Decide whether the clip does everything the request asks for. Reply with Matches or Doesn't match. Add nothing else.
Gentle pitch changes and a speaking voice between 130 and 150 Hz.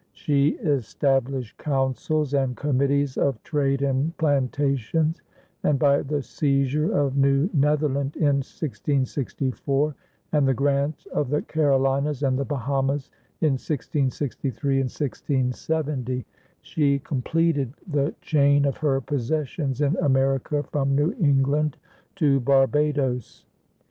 Matches